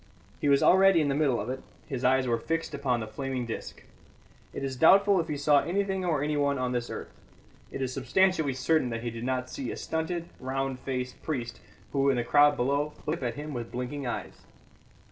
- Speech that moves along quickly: Yes, fast, 215 wpm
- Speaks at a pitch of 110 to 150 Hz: Yes, low, 135 Hz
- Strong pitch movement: No, average, 3.3 semitones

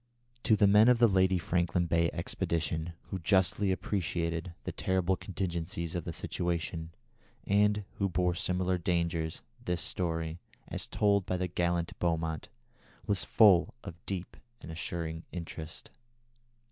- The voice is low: Yes, very low, 85 Hz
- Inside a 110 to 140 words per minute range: Yes, slow, 135 wpm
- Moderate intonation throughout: No, narrow, 2.1 semitones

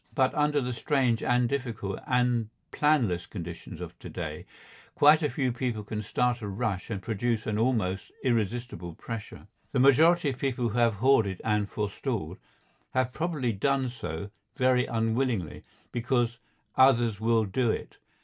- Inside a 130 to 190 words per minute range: Yes, average, 150 wpm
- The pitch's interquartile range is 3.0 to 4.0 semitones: Yes, average, 3.4 semitones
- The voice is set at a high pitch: No, low, 120 Hz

